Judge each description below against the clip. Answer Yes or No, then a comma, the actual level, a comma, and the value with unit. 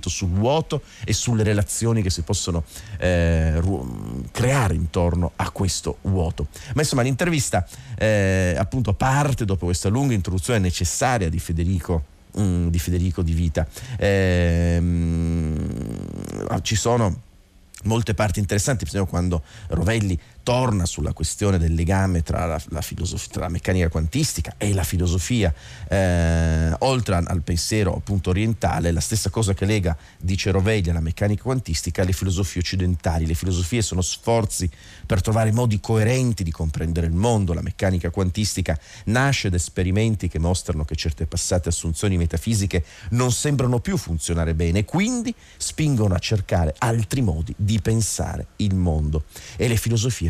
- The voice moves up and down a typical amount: Yes, average, 4.2 semitones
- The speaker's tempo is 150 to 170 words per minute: No, average, 140 wpm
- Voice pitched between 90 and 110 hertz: Yes, very low, 95 Hz